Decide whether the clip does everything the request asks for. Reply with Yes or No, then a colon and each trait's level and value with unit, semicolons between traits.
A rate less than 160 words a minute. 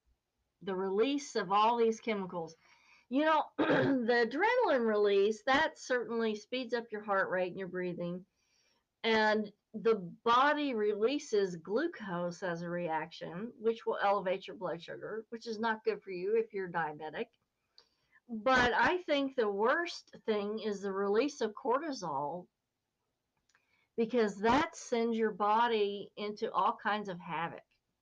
Yes: average, 140 wpm